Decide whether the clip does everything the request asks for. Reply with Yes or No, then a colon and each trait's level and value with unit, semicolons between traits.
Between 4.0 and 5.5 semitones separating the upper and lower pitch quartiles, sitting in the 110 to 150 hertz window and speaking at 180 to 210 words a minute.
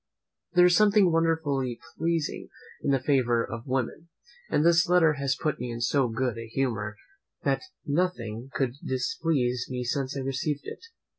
No: average, 4.9 semitones; low, 135 Hz; average, 160 wpm